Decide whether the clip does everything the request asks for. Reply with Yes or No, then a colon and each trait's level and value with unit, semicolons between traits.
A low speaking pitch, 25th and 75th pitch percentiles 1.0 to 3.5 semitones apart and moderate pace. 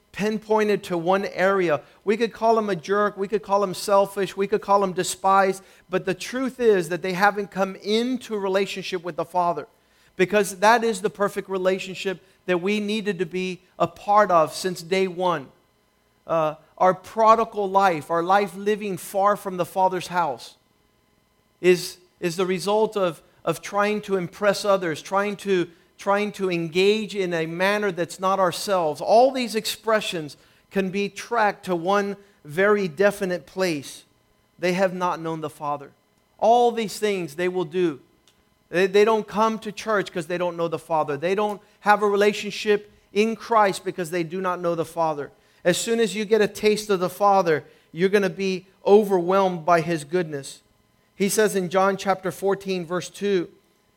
No: high, 195 Hz; narrow, 2.5 semitones; average, 175 wpm